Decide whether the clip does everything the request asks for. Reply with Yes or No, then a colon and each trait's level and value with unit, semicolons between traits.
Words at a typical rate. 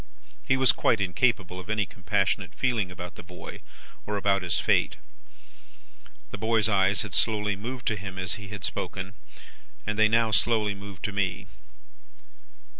Yes: average, 160 wpm